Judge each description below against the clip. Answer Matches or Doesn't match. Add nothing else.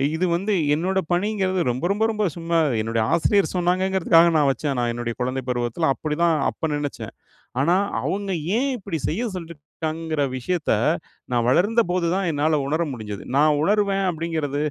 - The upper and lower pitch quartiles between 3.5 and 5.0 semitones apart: Matches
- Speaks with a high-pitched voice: Doesn't match